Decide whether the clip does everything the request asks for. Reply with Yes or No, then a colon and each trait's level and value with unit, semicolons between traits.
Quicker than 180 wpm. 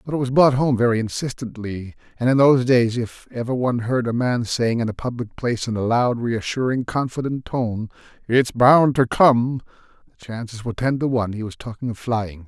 Yes: fast, 205 wpm